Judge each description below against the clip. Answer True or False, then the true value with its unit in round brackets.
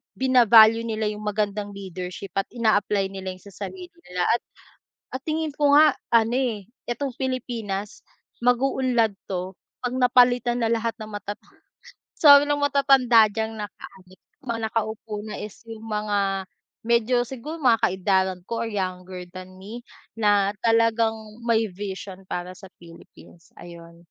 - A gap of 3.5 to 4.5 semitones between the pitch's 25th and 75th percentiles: True (3.9 semitones)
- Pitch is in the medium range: False (220 Hz)